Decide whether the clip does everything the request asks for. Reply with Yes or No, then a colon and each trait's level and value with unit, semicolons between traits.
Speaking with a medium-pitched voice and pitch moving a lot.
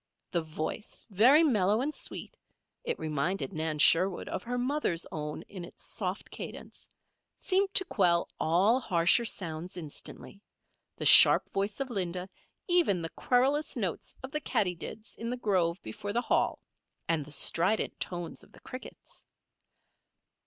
No: high, 195 Hz; wide, 6.6 semitones